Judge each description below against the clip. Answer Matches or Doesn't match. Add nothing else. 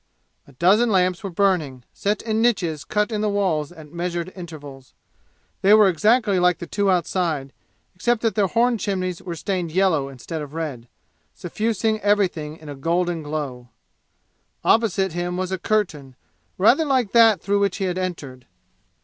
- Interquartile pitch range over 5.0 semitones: Doesn't match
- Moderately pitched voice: Matches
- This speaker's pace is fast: Doesn't match